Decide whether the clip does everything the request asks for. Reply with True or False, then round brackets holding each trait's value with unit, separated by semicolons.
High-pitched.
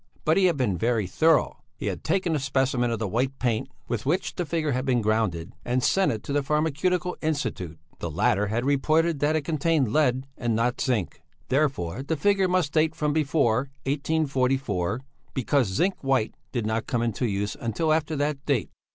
False (135 Hz)